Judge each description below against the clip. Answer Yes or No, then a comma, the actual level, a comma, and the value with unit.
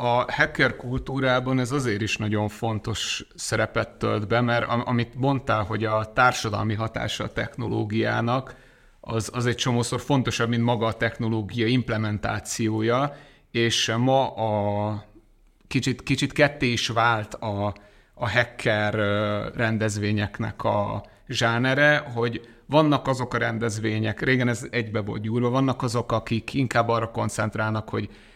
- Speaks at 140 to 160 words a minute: No, average, 130 wpm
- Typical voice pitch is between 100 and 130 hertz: Yes, low, 115 Hz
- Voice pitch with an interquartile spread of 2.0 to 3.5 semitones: Yes, narrow, 2.4 semitones